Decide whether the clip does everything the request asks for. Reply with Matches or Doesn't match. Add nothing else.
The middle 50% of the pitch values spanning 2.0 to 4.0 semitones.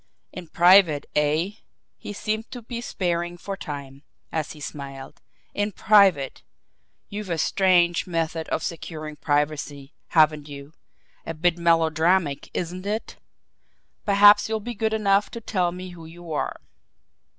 Doesn't match